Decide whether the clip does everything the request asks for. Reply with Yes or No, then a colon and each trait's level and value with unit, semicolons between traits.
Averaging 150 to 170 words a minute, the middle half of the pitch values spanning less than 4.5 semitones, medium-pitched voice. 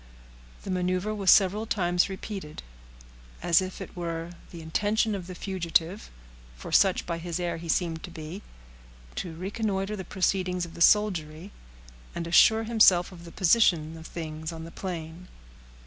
Yes: average, 160 wpm; average, 2.7 semitones; medium, 180 Hz